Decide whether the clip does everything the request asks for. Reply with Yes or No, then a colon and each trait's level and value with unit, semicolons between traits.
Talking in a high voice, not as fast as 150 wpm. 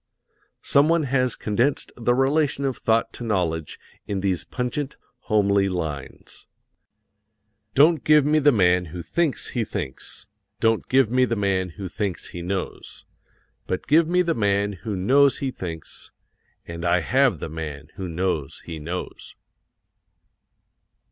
No: low, 105 Hz; average, 140 wpm